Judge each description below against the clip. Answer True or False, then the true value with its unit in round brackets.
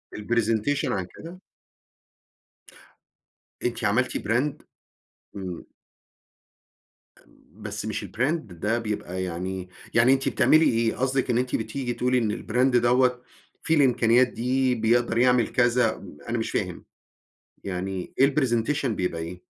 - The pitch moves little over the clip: False (3.6 semitones)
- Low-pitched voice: True (120 Hz)